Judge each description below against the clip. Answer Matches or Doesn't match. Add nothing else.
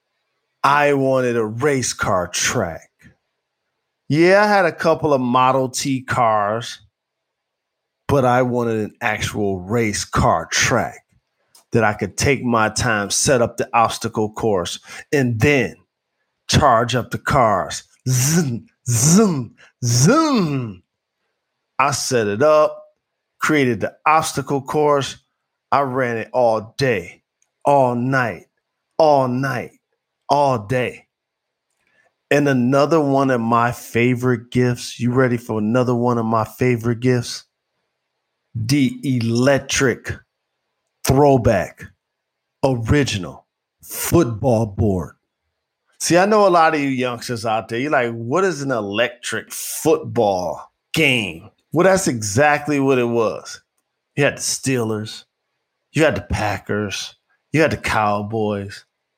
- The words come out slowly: Matches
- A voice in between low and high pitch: Doesn't match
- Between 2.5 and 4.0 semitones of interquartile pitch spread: Matches